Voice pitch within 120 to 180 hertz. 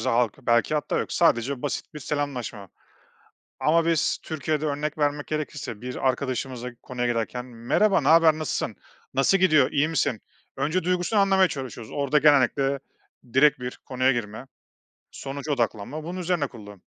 Yes: medium, 140 Hz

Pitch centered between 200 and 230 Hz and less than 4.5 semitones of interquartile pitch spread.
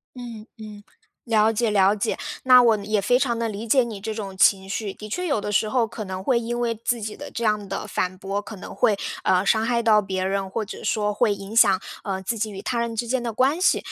Yes: high, 215 Hz; average, 2.8 semitones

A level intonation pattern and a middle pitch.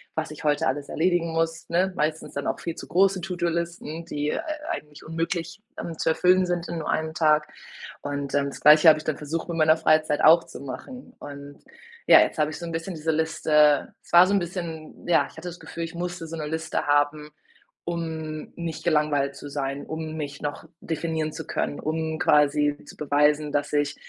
Yes: narrow, 2.1 semitones; medium, 160 Hz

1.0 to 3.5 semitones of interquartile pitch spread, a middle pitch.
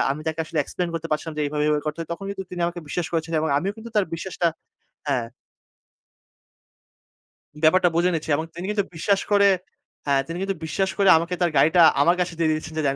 Yes: average, 2.9 semitones; medium, 170 Hz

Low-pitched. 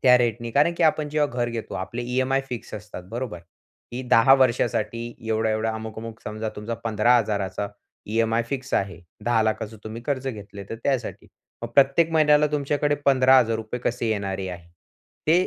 Yes: low, 115 Hz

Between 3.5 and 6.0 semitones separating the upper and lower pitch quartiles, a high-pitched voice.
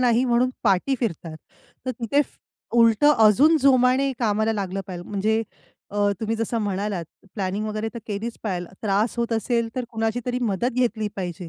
No: average, 3.1 semitones; high, 220 Hz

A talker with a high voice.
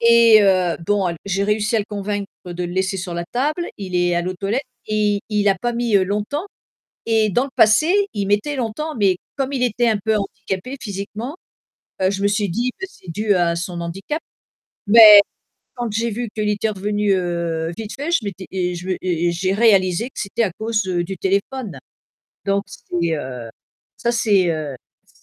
Yes: high, 205 Hz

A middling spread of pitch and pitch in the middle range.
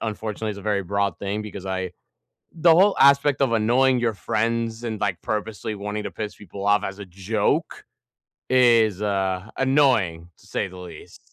No: average, 3.0 semitones; low, 105 Hz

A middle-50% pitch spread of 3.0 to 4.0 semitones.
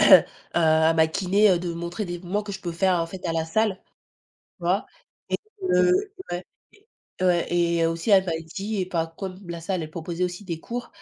No: narrow, 2.6 semitones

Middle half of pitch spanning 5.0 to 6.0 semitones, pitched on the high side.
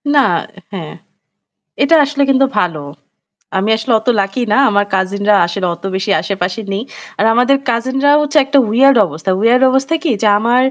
Yes: wide, 5.5 semitones; high, 230 Hz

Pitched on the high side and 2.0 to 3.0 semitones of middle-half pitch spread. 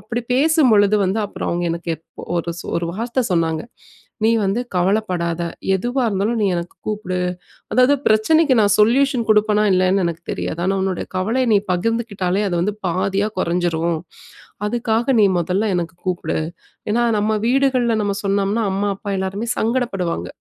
No: high, 205 Hz; average, 4.3 semitones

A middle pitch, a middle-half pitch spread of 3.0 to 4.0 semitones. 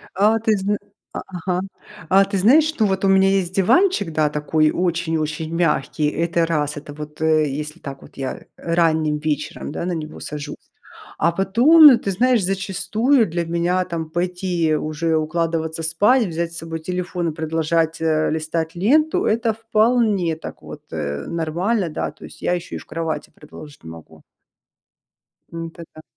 Yes: medium, 170 Hz; average, 3.6 semitones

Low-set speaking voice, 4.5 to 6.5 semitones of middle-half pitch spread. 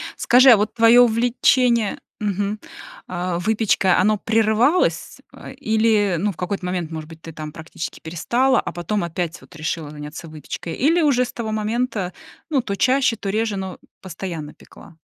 No: high, 205 Hz; average, 5.1 semitones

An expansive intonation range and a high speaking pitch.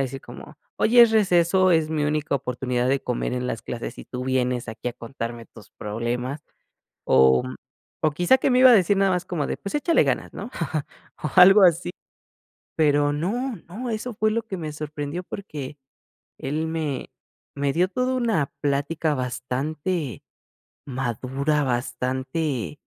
No: wide, 6.3 semitones; medium, 150 Hz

